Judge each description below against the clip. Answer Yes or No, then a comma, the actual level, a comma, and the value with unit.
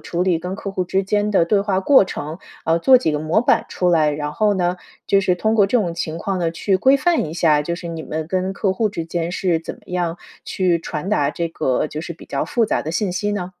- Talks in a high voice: No, medium, 180 Hz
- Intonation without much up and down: No, average, 3.2 semitones